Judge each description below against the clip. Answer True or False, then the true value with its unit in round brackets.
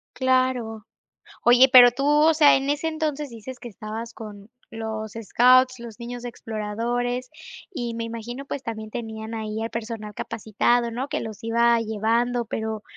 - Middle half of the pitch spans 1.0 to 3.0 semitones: True (2.4 semitones)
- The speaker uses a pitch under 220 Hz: False (235 Hz)